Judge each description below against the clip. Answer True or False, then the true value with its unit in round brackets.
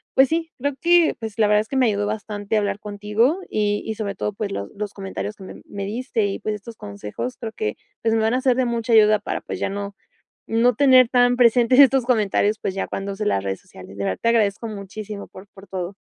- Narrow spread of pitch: False (3.2 semitones)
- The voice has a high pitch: True (215 Hz)